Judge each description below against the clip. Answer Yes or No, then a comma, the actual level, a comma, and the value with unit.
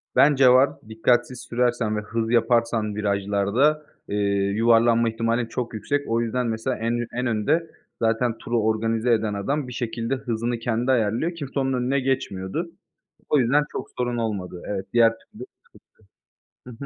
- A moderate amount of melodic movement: No, narrow, 2.2 semitones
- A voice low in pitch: Yes, low, 115 Hz